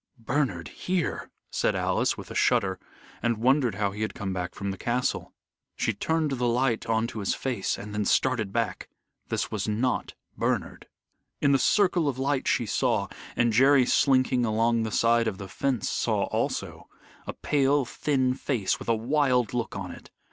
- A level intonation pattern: No, average, 3.7 semitones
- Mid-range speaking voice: No, low, 120 Hz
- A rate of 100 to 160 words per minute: No, average, 175 wpm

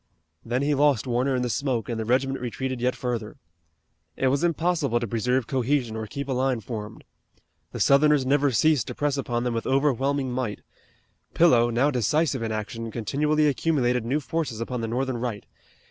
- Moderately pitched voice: No, low, 125 Hz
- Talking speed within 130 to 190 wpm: Yes, average, 180 wpm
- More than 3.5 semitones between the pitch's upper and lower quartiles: No, average, 3.1 semitones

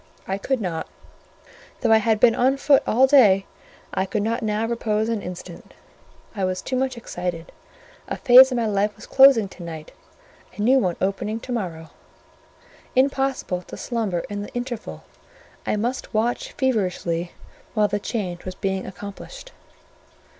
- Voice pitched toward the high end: Yes, high, 215 Hz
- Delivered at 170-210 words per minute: No, average, 160 wpm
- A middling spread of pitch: Yes, average, 4.5 semitones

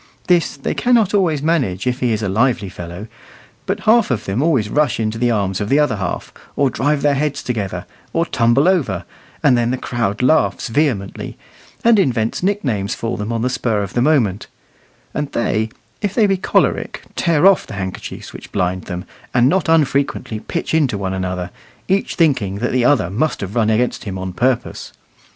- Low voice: Yes, low, 125 Hz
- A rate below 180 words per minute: No, average, 190 wpm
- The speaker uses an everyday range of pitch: No, wide, 6.7 semitones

